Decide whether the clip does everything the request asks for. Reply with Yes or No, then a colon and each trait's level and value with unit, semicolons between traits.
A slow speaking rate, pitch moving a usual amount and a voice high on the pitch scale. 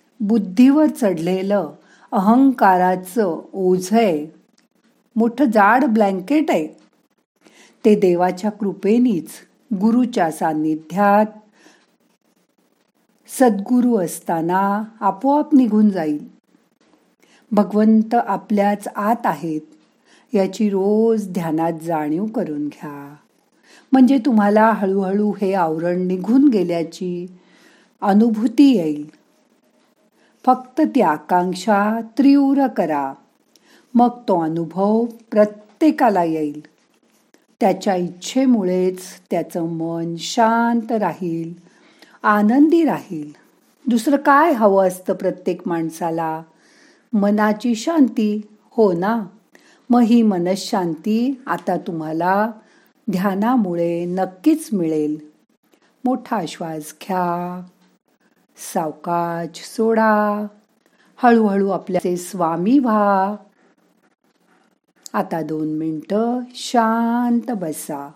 Yes: slow, 75 wpm; average, 5.0 semitones; high, 205 Hz